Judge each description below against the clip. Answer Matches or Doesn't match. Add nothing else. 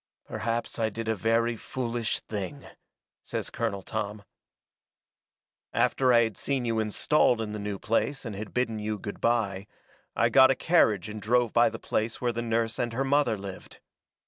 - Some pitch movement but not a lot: Doesn't match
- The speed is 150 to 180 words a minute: Matches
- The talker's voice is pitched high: Doesn't match